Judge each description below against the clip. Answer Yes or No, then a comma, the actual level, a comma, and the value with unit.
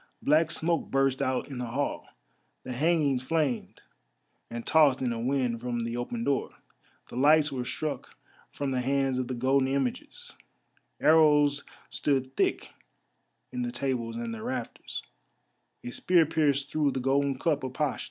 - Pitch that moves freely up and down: No, average, 2.9 semitones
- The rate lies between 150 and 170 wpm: Yes, average, 160 wpm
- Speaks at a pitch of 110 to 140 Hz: Yes, low, 135 Hz